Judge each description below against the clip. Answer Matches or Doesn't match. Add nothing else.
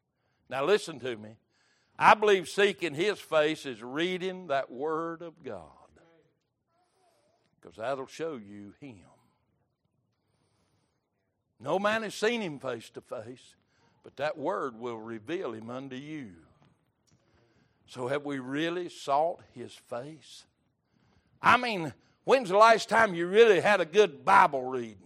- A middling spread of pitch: Doesn't match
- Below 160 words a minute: Matches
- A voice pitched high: Doesn't match